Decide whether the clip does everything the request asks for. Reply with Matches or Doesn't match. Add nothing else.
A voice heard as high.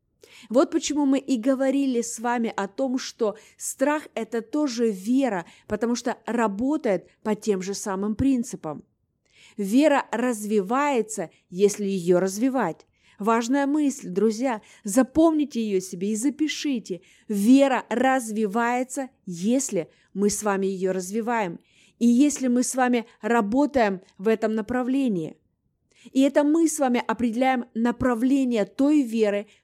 Matches